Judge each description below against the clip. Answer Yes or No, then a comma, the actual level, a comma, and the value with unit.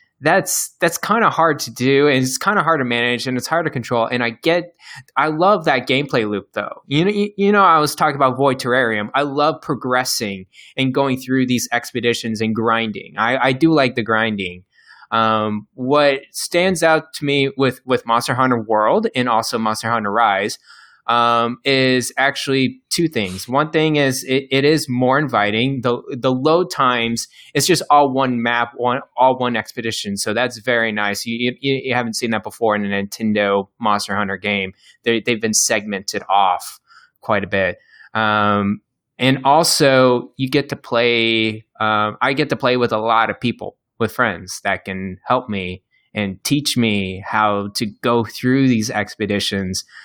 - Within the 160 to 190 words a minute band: Yes, average, 185 wpm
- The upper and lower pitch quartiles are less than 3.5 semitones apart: No, average, 3.9 semitones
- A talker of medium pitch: No, low, 120 Hz